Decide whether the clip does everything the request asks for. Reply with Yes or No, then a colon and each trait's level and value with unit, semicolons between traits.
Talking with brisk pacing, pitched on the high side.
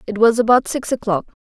Yes: fast, 210 wpm; high, 225 Hz